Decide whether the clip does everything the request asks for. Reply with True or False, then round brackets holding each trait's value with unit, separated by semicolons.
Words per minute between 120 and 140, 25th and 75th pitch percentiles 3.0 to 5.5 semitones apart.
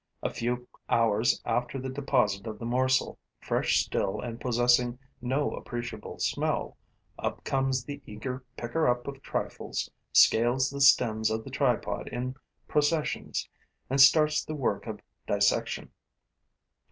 False (135 wpm; 2.5 semitones)